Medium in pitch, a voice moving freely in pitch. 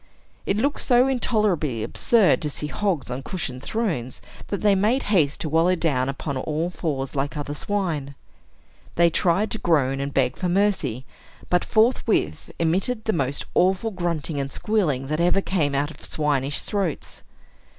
Yes: medium, 165 Hz; wide, 6.3 semitones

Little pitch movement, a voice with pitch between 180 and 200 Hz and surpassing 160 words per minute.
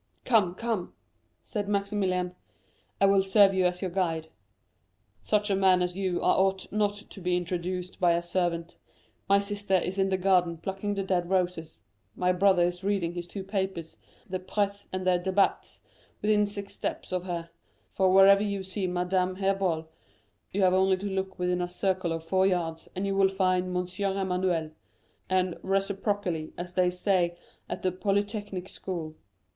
Yes: narrow, 1.7 semitones; medium, 185 Hz; average, 170 wpm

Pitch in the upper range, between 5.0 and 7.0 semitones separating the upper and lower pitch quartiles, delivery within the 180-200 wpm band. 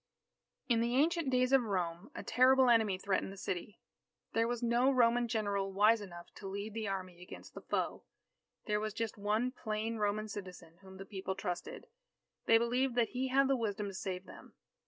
No: high, 215 Hz; average, 3.8 semitones; average, 195 wpm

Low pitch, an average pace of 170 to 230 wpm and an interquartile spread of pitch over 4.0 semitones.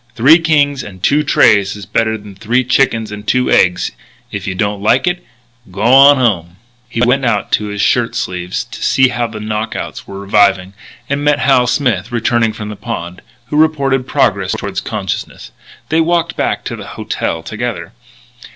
Yes: low, 115 Hz; average, 180 wpm; average, 4.7 semitones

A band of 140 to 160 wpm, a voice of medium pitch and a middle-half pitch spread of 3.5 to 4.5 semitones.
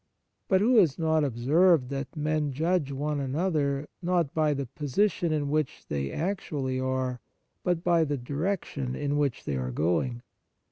Yes: average, 155 wpm; medium, 145 Hz; average, 3.9 semitones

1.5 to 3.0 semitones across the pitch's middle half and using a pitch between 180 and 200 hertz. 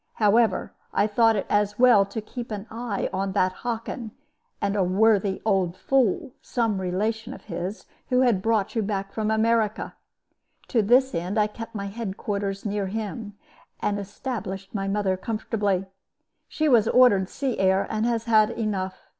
No: narrow, 2.6 semitones; high, 210 Hz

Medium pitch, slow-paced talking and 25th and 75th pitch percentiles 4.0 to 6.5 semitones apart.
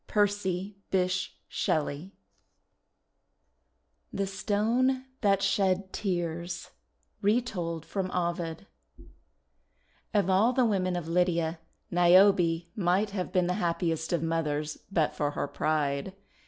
No: medium, 180 Hz; slow, 105 wpm; average, 3.1 semitones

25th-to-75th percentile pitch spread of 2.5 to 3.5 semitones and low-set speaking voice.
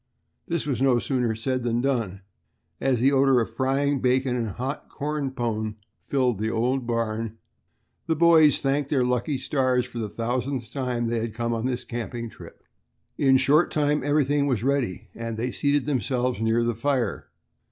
Yes: average, 3.0 semitones; low, 125 Hz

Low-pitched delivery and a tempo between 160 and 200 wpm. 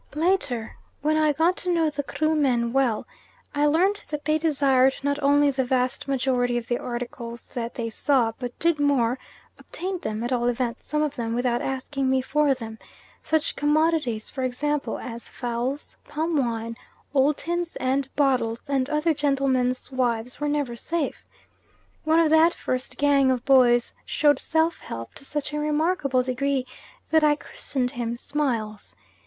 No: very high, 270 Hz; average, 165 wpm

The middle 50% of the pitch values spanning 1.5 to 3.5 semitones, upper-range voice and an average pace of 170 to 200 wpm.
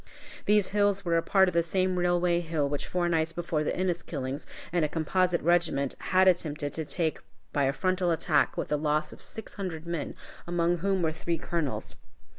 No: average, 2.7 semitones; medium, 170 Hz; average, 195 wpm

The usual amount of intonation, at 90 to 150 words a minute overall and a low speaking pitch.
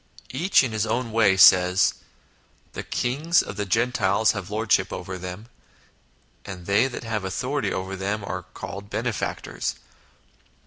Yes: average, 3.7 semitones; average, 145 wpm; low, 105 Hz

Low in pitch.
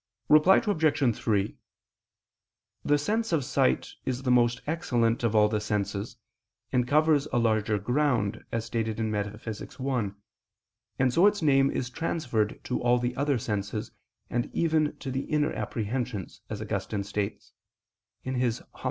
Yes: low, 120 Hz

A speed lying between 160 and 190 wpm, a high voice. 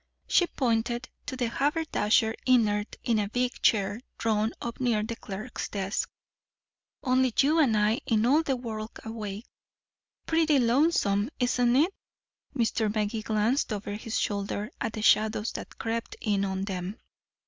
No: average, 150 wpm; high, 225 Hz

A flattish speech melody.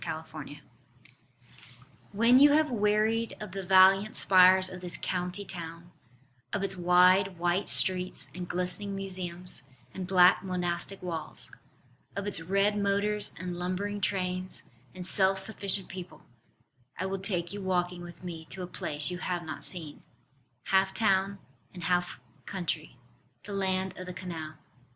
Yes: narrow, 1.8 semitones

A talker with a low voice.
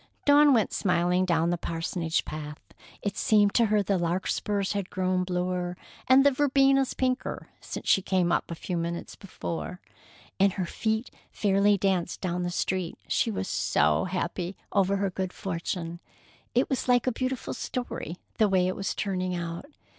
No: medium, 185 Hz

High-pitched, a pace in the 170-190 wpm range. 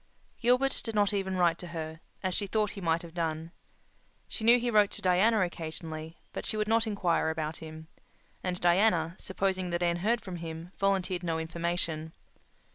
No: medium, 175 Hz; average, 185 wpm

